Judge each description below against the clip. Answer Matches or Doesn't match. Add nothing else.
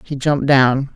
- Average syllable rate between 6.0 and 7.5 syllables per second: Doesn't match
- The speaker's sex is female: Matches